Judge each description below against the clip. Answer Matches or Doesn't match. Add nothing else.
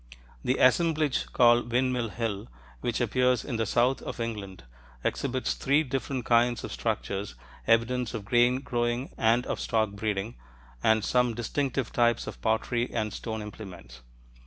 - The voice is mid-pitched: Doesn't match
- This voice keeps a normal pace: Matches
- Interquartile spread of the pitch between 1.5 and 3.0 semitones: Matches